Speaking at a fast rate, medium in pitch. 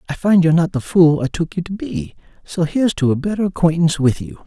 Yes: fast, 255 wpm; medium, 165 Hz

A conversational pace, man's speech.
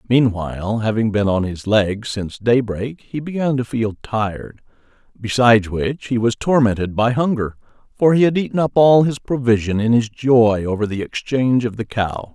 Yes: average, 180 wpm; male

